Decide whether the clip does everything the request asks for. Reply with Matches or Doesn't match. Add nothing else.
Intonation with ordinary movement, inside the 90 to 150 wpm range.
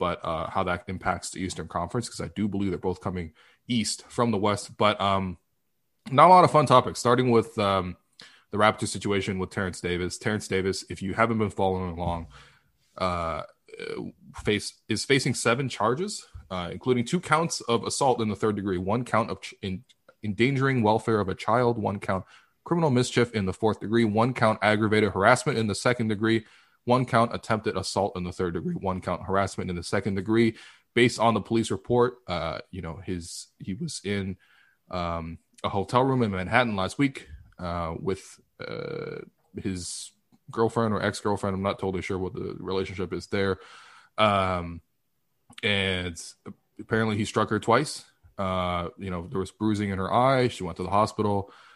Doesn't match